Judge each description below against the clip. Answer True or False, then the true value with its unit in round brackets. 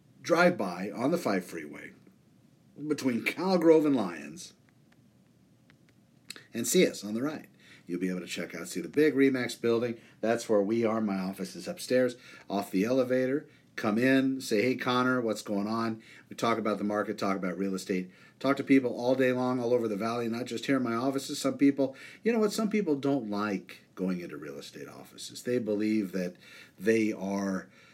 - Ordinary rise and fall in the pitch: True (4.6 semitones)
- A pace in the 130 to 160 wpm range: False (195 wpm)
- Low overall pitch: True (115 Hz)